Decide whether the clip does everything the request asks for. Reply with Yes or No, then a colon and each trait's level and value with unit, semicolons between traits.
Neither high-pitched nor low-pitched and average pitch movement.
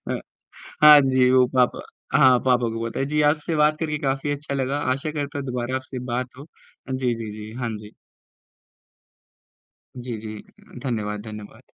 No: low, 130 Hz; average, 3.3 semitones